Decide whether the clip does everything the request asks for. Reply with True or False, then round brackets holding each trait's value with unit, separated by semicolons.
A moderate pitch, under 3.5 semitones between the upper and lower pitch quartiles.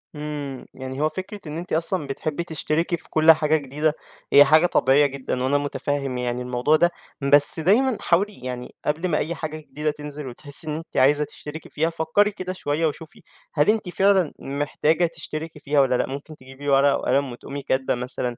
True (150 Hz; 2.8 semitones)